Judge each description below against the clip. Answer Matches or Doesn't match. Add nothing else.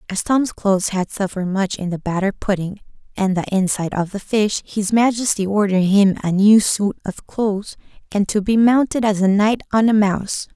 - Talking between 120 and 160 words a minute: Doesn't match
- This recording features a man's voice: Doesn't match